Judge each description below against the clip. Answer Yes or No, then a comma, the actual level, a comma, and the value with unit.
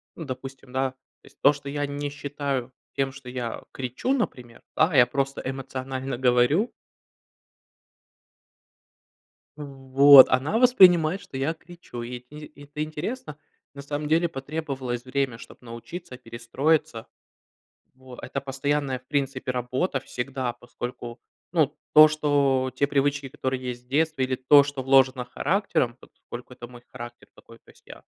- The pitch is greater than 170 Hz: No, low, 135 Hz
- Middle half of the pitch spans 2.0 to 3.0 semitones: Yes, narrow, 2.6 semitones